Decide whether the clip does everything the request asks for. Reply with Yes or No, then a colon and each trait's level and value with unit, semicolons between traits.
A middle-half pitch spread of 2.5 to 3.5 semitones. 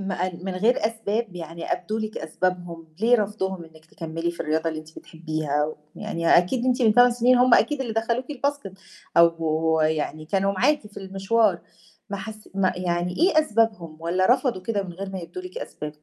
No: average, 5.3 semitones